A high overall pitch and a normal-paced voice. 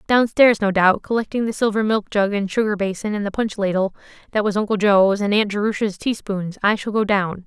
No: high, 205 Hz; fast, 215 wpm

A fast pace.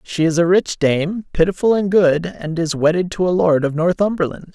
Yes: fast, 210 wpm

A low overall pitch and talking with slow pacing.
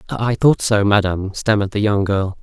No: low, 105 Hz; average, 200 wpm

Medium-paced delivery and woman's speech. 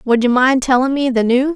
No: fast, 270 wpm; female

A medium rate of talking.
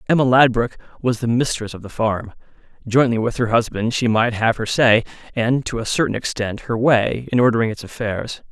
Yes: average, 195 wpm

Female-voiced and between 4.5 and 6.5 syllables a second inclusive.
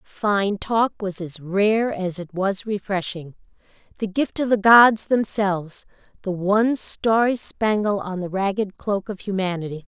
No: female; 4.1 syllables/s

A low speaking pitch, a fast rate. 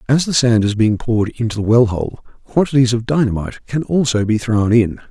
Yes: low, 115 Hz; fast, 210 wpm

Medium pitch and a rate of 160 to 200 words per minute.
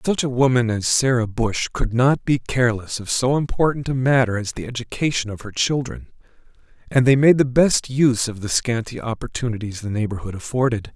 No: low, 120 Hz; average, 185 wpm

